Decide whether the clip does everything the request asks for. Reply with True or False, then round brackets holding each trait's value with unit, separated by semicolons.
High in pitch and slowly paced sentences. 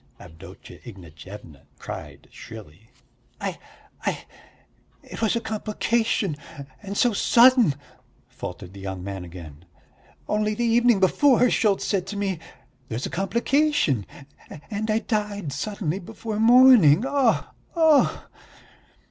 True (205 Hz; 115 wpm)